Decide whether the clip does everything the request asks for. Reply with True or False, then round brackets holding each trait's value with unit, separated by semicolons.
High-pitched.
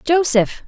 True (285 Hz)